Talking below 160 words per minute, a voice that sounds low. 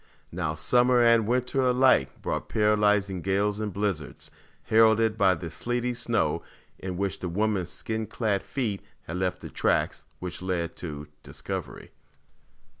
Yes: average, 140 wpm; low, 105 Hz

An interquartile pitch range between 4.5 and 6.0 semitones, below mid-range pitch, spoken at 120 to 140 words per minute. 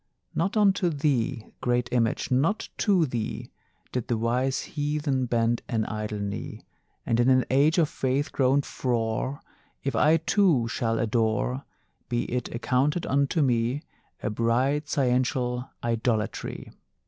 No: average, 3.7 semitones; low, 125 Hz; slow, 135 wpm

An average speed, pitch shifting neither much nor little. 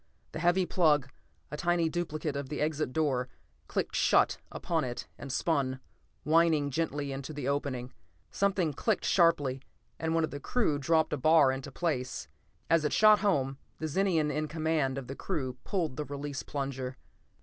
Yes: average, 170 wpm; average, 3.3 semitones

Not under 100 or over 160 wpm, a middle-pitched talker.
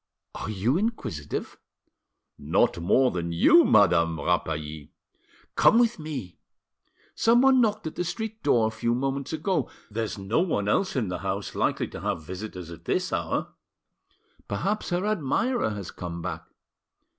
No: average, 145 wpm; low, 115 Hz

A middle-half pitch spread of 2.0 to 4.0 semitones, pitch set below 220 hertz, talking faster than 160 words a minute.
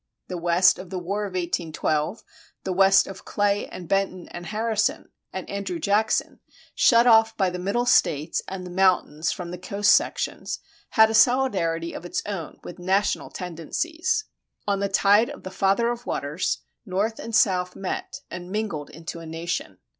Yes: average, 3.4 semitones; high, 190 Hz; average, 170 wpm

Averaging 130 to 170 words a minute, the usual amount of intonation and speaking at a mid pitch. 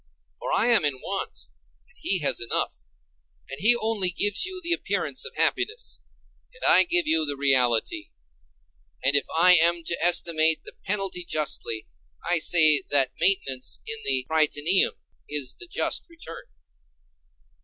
No: average, 150 wpm; wide, 6.9 semitones; medium, 170 Hz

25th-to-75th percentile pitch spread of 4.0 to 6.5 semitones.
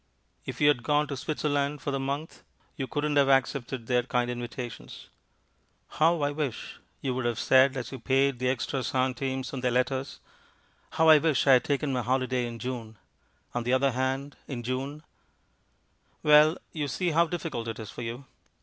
No: average, 2.7 semitones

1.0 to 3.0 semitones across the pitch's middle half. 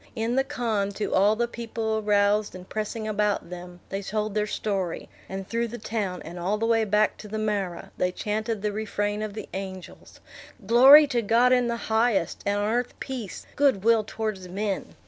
Yes: narrow, 2.5 semitones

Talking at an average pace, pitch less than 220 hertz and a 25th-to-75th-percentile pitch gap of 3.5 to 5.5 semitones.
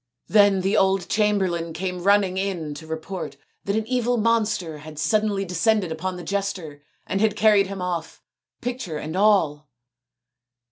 Yes: average, 150 wpm; high, 190 Hz; average, 3.9 semitones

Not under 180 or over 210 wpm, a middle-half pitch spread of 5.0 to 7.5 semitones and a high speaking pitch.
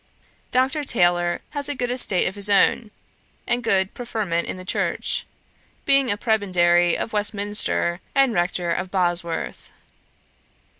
No: slow, 135 wpm; wide, 5.5 semitones; high, 200 Hz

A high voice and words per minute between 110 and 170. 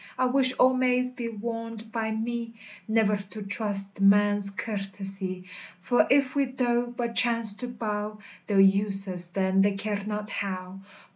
Yes: high, 210 Hz; average, 155 wpm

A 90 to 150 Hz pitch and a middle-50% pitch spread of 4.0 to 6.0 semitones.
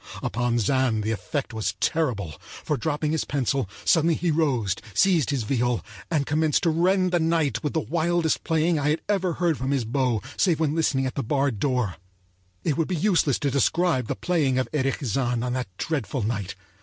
Yes: medium, 140 Hz; average, 4.9 semitones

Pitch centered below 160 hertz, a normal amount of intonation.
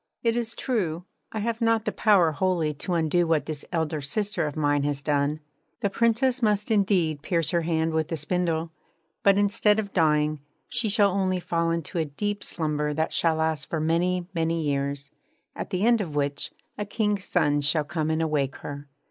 No: medium, 165 Hz; average, 4.9 semitones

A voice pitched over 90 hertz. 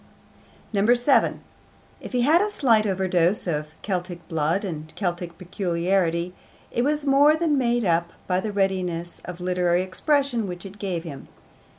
Yes: medium, 185 Hz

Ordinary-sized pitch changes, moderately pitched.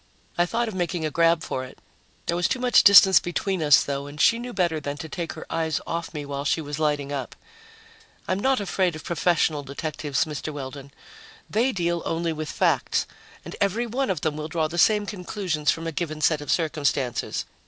Yes: average, 3.8 semitones; medium, 165 Hz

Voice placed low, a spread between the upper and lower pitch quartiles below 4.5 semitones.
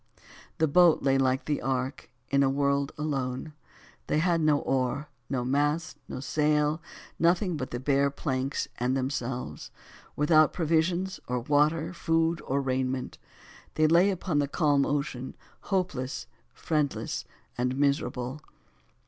No: medium, 145 Hz; average, 3.1 semitones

